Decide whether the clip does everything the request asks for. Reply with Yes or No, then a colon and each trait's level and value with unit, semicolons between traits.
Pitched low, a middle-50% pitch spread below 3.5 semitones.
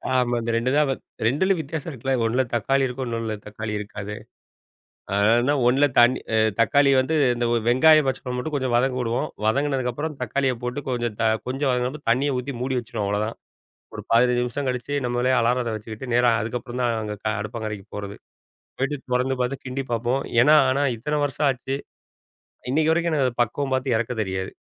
Yes: low, 125 Hz; average, 2.9 semitones